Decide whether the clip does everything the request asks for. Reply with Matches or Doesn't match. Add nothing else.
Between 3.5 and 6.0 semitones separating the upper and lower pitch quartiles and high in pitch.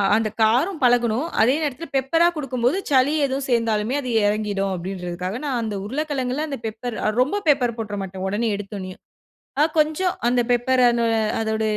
Matches